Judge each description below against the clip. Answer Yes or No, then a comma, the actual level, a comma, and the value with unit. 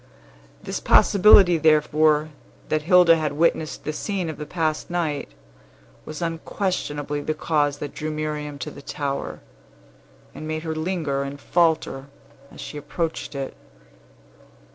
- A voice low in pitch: No, medium, 155 Hz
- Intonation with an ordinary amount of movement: No, narrow, 2.1 semitones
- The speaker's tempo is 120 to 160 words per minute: Yes, slow, 135 wpm